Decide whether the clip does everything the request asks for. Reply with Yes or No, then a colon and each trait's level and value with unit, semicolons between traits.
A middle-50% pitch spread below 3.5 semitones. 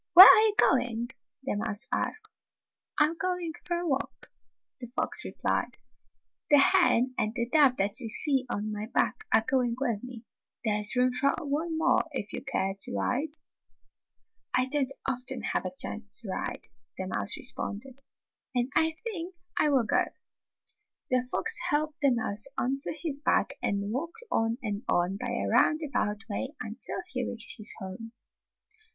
No: average, 5.3 semitones